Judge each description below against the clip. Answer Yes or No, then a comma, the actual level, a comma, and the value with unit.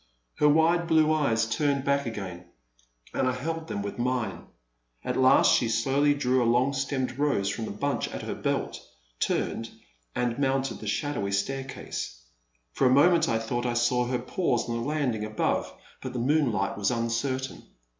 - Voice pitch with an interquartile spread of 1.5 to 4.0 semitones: Yes, average, 3.7 semitones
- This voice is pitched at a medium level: No, low, 125 Hz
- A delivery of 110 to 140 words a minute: No, average, 175 wpm